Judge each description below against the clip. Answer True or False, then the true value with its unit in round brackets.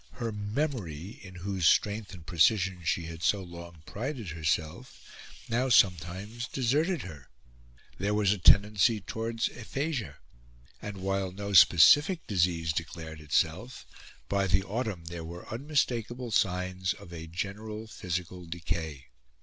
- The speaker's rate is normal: False (130 wpm)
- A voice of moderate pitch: False (95 Hz)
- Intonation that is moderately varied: True (4.6 semitones)